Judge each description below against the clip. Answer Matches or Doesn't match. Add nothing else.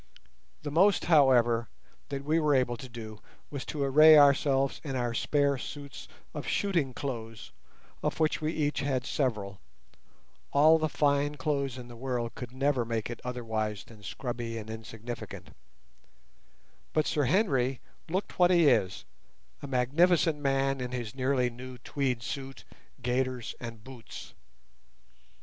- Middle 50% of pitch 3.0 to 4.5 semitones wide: Matches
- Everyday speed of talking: Matches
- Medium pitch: Doesn't match